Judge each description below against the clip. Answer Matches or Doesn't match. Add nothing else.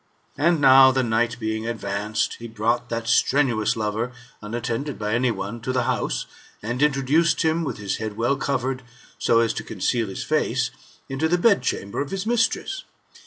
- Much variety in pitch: Doesn't match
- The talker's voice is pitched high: Doesn't match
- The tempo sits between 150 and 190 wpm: Matches